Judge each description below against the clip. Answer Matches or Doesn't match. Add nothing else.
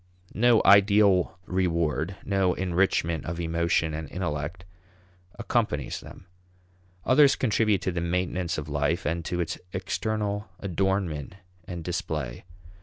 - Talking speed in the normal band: Doesn't match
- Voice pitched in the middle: Doesn't match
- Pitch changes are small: Doesn't match